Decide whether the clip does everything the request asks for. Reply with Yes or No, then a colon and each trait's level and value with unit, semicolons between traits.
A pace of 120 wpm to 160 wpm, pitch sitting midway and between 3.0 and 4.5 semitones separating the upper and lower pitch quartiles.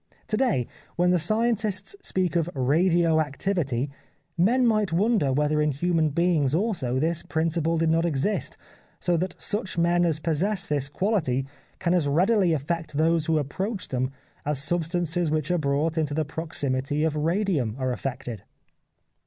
Yes: average, 155 wpm; medium, 165 Hz; average, 3.7 semitones